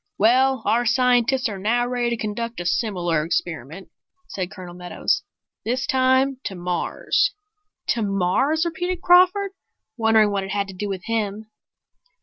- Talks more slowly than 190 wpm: Yes, average, 145 wpm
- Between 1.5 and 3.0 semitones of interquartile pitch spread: No, average, 5.1 semitones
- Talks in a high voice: Yes, high, 225 Hz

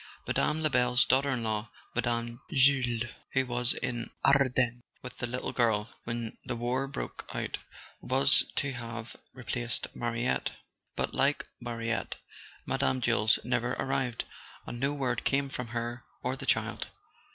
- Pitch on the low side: Yes, low, 120 Hz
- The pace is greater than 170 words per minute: No, average, 145 wpm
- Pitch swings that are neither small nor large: No, narrow, 2.0 semitones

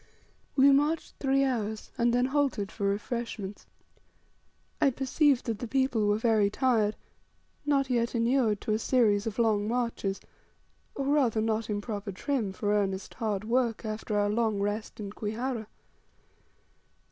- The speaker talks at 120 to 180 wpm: Yes, average, 145 wpm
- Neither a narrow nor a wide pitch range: Yes, average, 3.6 semitones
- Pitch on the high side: Yes, high, 225 Hz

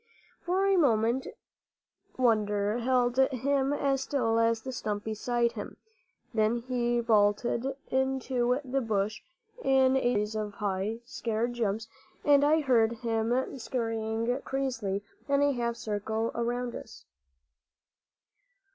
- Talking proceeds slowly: Yes, slow, 120 wpm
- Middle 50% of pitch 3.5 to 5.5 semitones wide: No, average, 3.1 semitones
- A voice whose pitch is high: Yes, high, 235 Hz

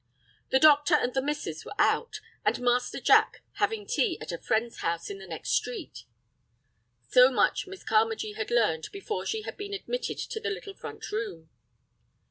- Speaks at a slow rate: No, average, 175 wpm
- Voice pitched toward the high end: Yes, very high, 270 Hz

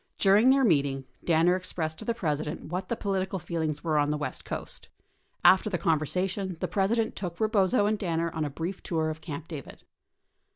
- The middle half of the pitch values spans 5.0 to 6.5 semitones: No, average, 3.8 semitones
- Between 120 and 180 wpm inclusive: No, average, 195 wpm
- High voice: No, medium, 175 Hz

